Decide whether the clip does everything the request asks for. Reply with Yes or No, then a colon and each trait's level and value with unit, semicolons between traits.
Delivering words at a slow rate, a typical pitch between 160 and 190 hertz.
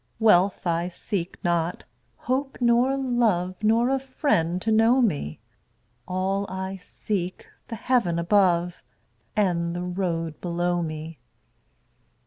Yes: slow, 115 wpm; medium, 185 Hz